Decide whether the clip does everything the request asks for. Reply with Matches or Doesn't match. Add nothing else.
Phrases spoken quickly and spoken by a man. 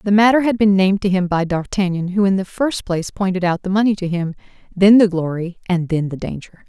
Doesn't match